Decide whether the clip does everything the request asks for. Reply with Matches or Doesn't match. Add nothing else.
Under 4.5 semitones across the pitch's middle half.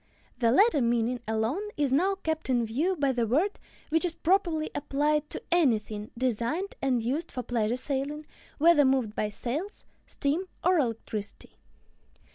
Doesn't match